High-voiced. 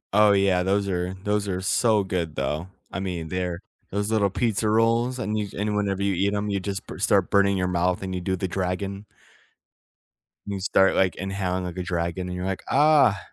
No: very low, 95 Hz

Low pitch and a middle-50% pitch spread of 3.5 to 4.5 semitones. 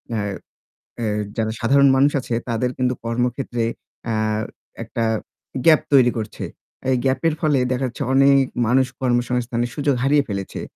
No: low, 125 Hz; average, 2.7 semitones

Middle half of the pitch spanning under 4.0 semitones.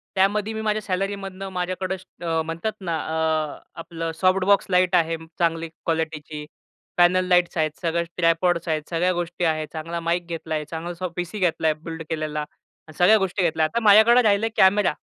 Yes: average, 2.7 semitones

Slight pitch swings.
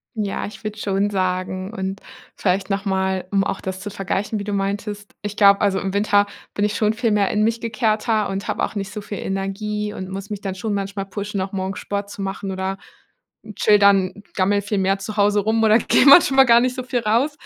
Yes: narrow, 1.5 semitones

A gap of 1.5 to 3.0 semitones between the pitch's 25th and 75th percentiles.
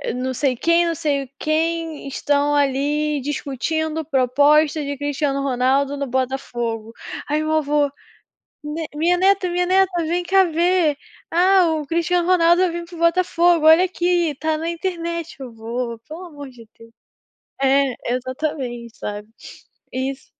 No: average, 3.9 semitones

